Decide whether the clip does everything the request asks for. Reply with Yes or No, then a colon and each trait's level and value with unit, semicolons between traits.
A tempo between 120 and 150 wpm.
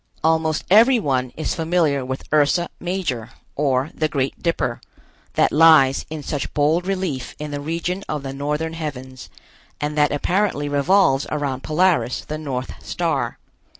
Yes: average, 145 wpm